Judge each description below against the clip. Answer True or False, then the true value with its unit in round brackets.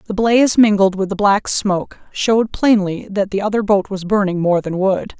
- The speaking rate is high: True (210 wpm)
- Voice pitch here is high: True (200 Hz)